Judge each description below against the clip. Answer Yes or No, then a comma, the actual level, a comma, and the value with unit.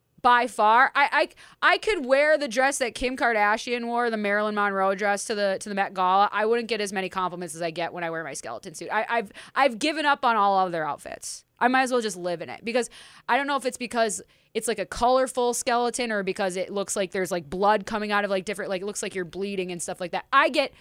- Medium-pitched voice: No, high, 215 Hz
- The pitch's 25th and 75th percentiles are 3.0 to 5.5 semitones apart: Yes, average, 4.3 semitones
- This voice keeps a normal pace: No, fast, 270 wpm